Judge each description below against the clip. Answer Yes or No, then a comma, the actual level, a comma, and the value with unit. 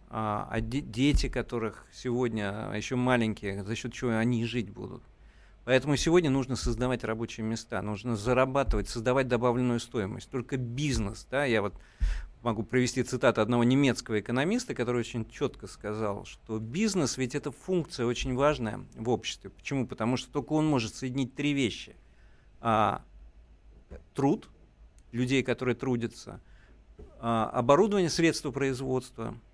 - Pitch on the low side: Yes, low, 120 Hz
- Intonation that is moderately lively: Yes, average, 3.3 semitones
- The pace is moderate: Yes, average, 130 wpm